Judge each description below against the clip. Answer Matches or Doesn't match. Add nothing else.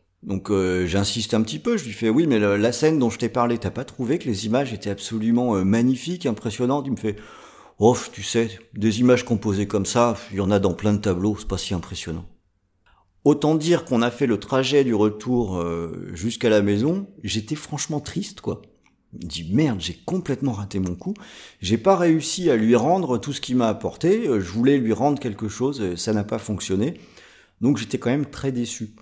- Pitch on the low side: Matches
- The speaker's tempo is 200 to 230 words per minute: Matches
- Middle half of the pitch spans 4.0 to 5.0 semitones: Matches